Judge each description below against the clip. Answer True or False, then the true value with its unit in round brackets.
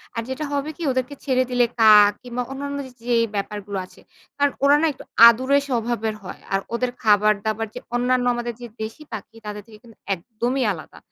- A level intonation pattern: False (3.2 semitones)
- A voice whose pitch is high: True (240 Hz)